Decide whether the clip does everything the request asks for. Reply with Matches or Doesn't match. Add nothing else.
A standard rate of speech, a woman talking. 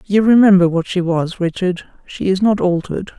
Matches